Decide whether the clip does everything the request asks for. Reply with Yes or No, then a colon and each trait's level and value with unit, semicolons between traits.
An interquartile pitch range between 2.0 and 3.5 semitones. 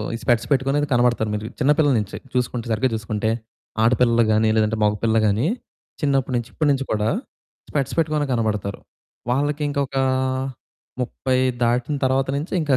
No: average, 3.9 semitones